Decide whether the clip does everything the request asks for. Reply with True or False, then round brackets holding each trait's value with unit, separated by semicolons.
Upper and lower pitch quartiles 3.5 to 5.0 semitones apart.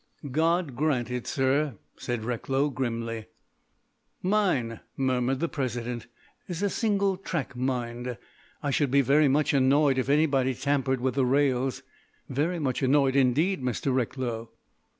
False (3.0 semitones)